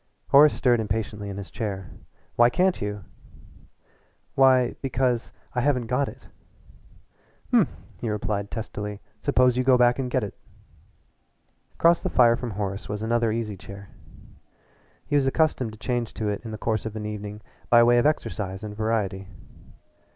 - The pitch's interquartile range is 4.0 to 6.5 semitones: No, average, 3.3 semitones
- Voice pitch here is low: Yes, low, 115 Hz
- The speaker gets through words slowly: No, average, 160 wpm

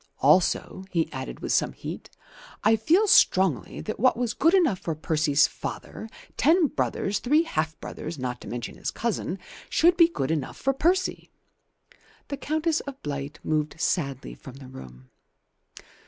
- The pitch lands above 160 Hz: Yes, medium, 185 Hz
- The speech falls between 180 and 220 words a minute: No, average, 155 wpm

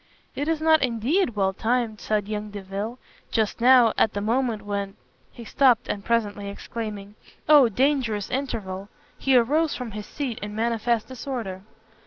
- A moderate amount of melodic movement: Yes, average, 3.7 semitones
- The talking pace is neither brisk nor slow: Yes, average, 160 wpm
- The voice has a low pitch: No, high, 225 Hz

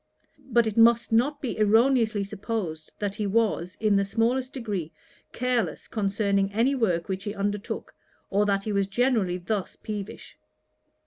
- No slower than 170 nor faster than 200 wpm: No, average, 150 wpm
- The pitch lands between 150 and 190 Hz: No, high, 210 Hz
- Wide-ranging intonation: No, average, 2.7 semitones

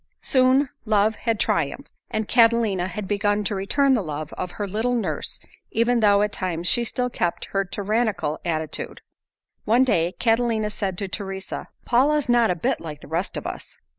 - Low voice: No, high, 210 Hz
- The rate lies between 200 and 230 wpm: No, average, 175 wpm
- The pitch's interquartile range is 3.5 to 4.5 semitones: Yes, average, 4.2 semitones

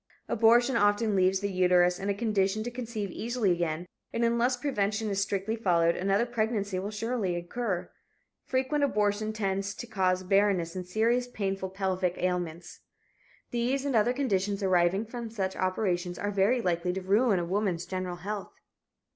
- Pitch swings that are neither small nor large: Yes, average, 3.7 semitones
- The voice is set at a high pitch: Yes, high, 200 Hz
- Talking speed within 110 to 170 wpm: Yes, average, 160 wpm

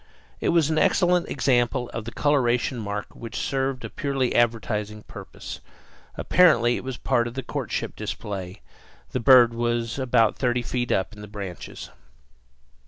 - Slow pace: No, average, 155 wpm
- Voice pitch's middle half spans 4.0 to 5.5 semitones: No, average, 2.9 semitones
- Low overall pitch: Yes, low, 120 Hz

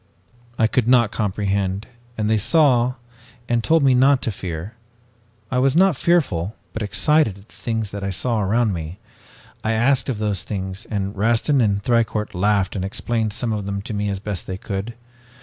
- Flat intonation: No, average, 3.4 semitones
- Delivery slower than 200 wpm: Yes, average, 185 wpm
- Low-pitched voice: Yes, low, 110 Hz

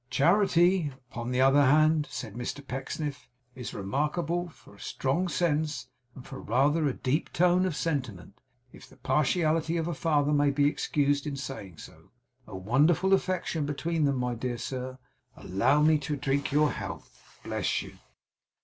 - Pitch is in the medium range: Yes, medium, 145 Hz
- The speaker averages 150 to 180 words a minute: Yes, average, 160 wpm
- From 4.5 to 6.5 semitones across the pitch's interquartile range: No, average, 3.7 semitones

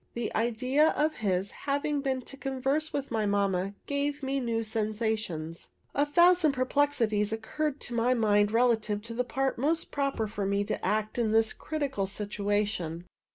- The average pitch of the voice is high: Yes, high, 230 Hz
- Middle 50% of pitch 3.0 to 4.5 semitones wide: No, average, 4.9 semitones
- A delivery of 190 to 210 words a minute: No, average, 160 wpm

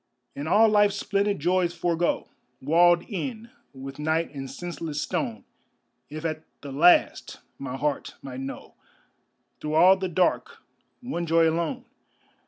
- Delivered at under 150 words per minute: Yes, slow, 135 wpm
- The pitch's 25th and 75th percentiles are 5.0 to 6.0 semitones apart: No, average, 4.0 semitones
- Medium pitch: Yes, medium, 165 Hz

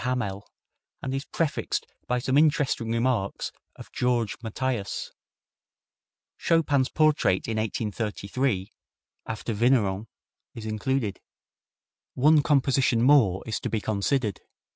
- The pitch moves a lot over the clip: No, average, 4.0 semitones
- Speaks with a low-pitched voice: Yes, low, 120 Hz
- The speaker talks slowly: Yes, slow, 105 wpm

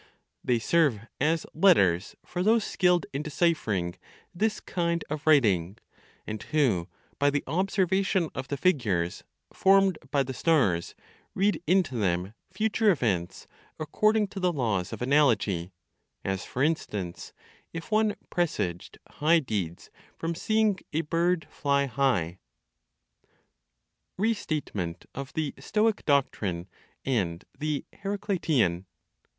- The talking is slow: Yes, slow, 120 wpm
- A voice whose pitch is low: No, medium, 145 Hz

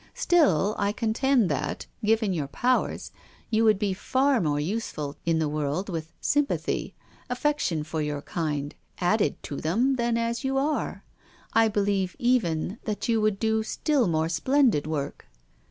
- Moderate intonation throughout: No, wide, 7.0 semitones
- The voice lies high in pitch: Yes, high, 205 Hz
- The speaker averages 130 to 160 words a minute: Yes, average, 155 wpm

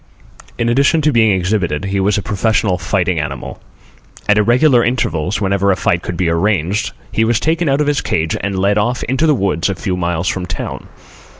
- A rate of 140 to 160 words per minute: No, average, 200 wpm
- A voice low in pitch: Yes, low, 100 Hz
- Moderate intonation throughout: Yes, average, 4.6 semitones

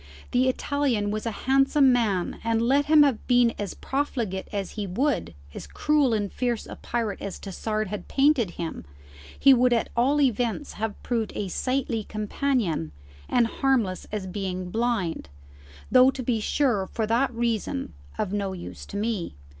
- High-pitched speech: Yes, high, 230 Hz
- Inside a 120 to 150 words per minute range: No, average, 165 wpm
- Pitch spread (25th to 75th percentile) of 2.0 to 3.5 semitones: No, average, 4.3 semitones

